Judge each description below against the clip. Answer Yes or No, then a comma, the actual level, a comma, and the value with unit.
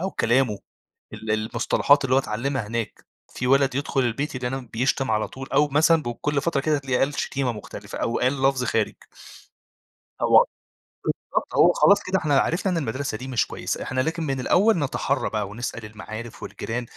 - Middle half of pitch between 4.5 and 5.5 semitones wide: No, average, 3.4 semitones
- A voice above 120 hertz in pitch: Yes, low, 130 Hz